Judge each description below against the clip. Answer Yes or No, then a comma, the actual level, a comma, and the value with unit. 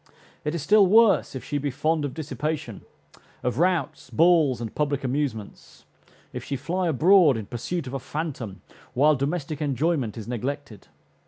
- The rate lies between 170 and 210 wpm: No, average, 160 wpm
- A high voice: No, medium, 145 Hz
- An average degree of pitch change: Yes, average, 4.3 semitones